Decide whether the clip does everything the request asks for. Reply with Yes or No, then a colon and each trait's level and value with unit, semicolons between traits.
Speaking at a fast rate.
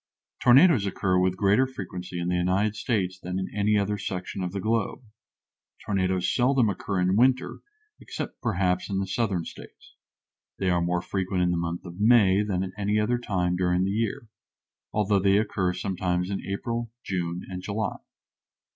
No: average, 175 wpm